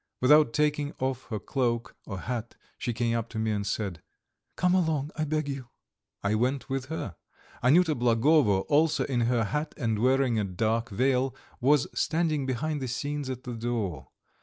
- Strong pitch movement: No, average, 4.4 semitones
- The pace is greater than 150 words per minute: Yes, average, 175 wpm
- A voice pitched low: Yes, low, 125 Hz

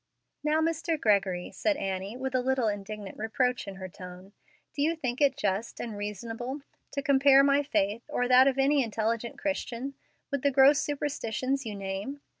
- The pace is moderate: Yes, average, 175 wpm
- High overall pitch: Yes, very high, 250 Hz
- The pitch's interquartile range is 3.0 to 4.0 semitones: No, average, 5.1 semitones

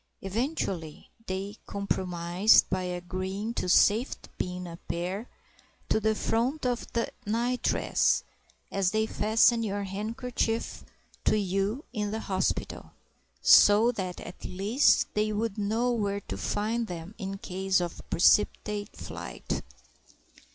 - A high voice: Yes, high, 205 Hz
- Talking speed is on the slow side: Yes, slow, 125 wpm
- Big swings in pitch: No, average, 3.1 semitones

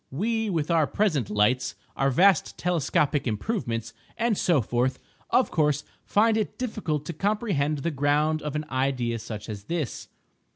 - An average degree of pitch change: No, wide, 6.5 semitones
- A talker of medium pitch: Yes, medium, 150 Hz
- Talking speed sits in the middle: Yes, average, 155 wpm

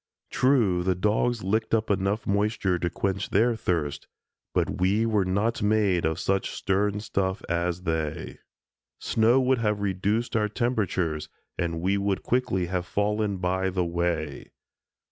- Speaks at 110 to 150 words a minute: Yes, average, 145 wpm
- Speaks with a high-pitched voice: No, low, 100 Hz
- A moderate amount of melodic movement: Yes, average, 3.2 semitones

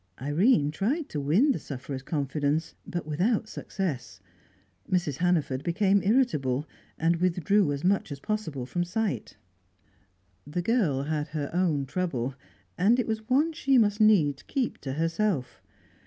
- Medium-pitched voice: Yes, medium, 170 Hz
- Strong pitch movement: Yes, wide, 6.7 semitones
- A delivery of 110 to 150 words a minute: Yes, average, 140 wpm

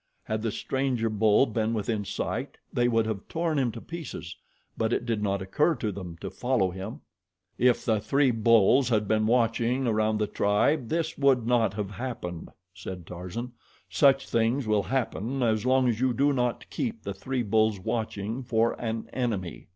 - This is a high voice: No, low, 115 Hz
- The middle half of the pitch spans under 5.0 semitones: Yes, average, 3.2 semitones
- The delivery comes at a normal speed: Yes, average, 180 wpm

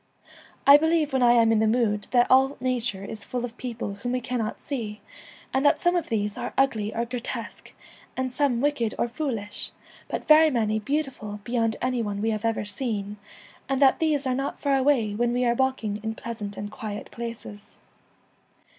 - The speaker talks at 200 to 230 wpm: Yes, fast, 205 wpm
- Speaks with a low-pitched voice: No, high, 240 Hz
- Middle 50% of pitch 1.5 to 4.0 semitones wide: Yes, average, 3.6 semitones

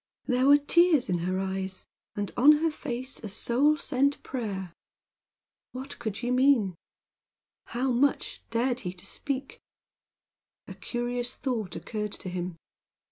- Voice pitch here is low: No, high, 245 Hz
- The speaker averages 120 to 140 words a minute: Yes, slow, 135 wpm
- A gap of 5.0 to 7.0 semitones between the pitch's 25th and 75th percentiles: Yes, wide, 5.4 semitones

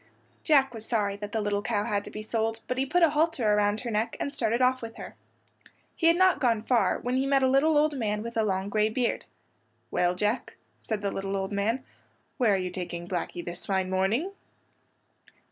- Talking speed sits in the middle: No, fast, 215 wpm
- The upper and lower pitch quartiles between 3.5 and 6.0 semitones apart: Yes, average, 4.3 semitones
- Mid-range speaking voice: No, high, 220 Hz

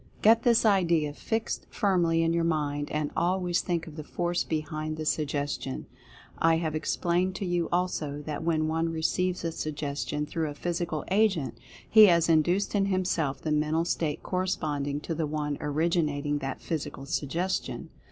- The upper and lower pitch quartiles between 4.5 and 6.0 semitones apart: No, average, 2.7 semitones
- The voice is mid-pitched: Yes, medium, 165 Hz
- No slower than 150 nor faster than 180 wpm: Yes, average, 160 wpm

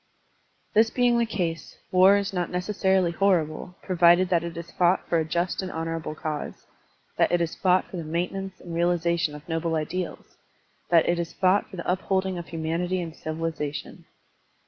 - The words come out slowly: No, average, 175 wpm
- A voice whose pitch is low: No, medium, 175 Hz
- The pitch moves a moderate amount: No, narrow, 2.2 semitones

